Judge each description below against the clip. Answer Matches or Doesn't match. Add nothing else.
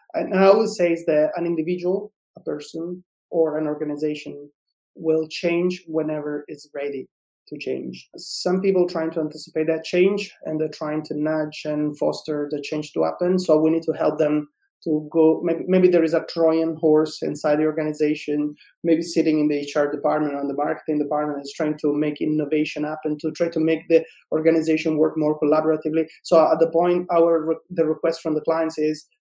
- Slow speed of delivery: Doesn't match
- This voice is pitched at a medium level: Matches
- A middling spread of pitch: Doesn't match